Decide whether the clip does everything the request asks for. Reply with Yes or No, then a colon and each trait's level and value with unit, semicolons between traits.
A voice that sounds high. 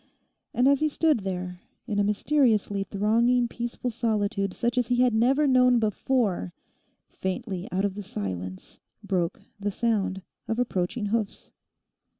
Yes: high, 215 Hz